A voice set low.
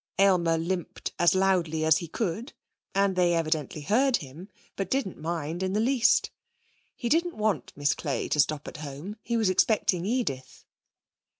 No: medium, 180 Hz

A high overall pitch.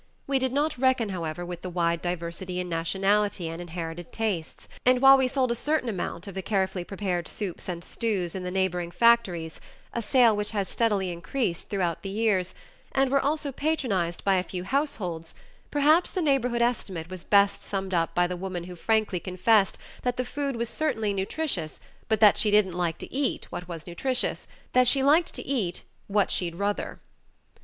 Yes: high, 200 Hz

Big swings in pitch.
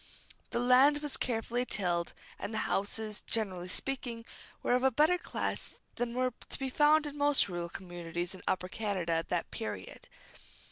Yes: wide, 6.5 semitones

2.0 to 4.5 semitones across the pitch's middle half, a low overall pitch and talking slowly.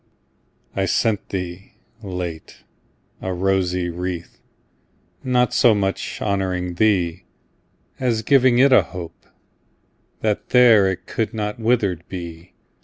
Yes: average, 3.6 semitones; very low, 95 Hz; slow, 110 wpm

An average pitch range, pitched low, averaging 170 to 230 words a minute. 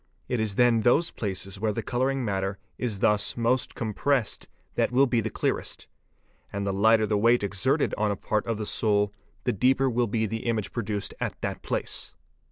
Yes: average, 3.1 semitones; low, 110 Hz; average, 195 wpm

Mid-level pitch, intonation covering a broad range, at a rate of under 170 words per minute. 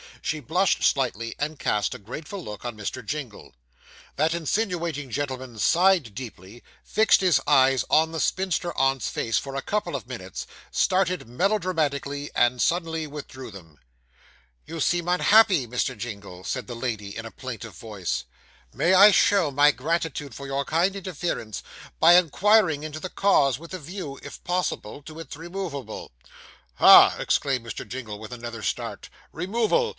Yes: medium, 145 Hz; wide, 6.4 semitones; average, 155 wpm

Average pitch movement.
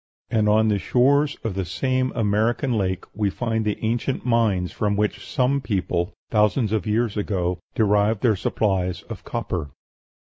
Yes: average, 3.2 semitones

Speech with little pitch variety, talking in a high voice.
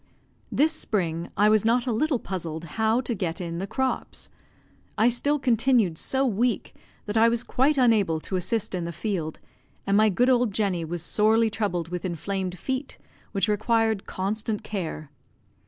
No: average, 4.7 semitones; high, 215 Hz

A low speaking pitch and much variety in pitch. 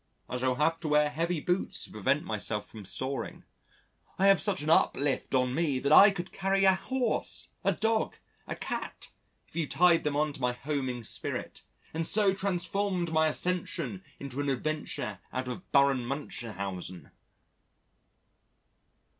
No: medium, 150 Hz; wide, 5.7 semitones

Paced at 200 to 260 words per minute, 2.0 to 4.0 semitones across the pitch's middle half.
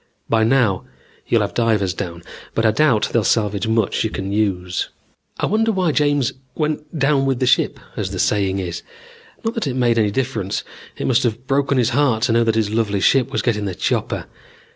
No: fast, 205 wpm; average, 4.7 semitones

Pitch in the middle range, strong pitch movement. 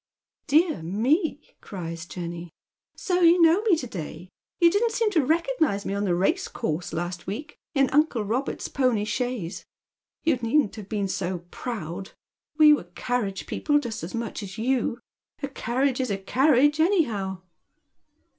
No: high, 240 Hz; wide, 7.9 semitones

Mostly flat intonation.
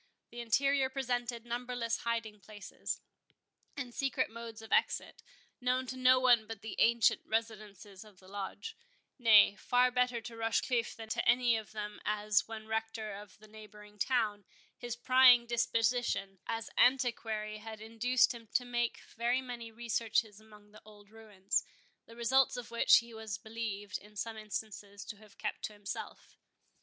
Yes: narrow, 2.3 semitones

